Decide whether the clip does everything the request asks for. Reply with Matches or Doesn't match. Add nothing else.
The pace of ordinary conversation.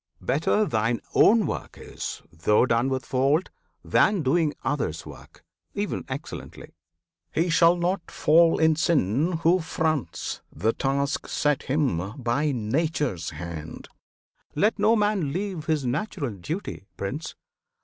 Doesn't match